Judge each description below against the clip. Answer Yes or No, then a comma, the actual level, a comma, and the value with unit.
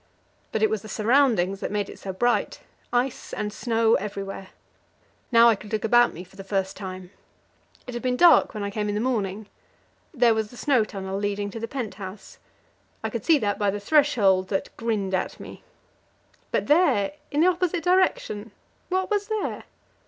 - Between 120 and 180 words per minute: No, average, 190 wpm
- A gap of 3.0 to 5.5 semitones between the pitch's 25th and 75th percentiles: Yes, average, 4.2 semitones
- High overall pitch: Yes, high, 215 Hz